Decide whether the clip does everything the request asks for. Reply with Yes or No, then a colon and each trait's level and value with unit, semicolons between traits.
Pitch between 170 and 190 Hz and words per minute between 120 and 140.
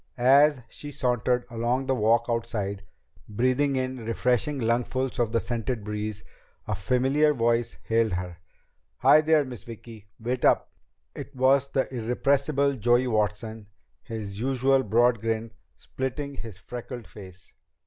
No: low, 120 Hz; slow, 135 wpm